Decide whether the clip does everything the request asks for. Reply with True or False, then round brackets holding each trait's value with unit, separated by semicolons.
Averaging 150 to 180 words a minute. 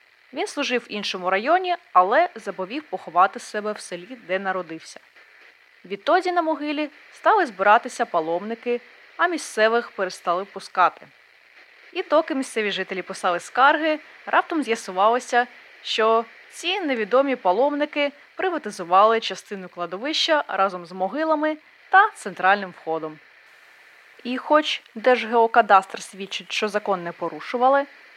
False (110 wpm)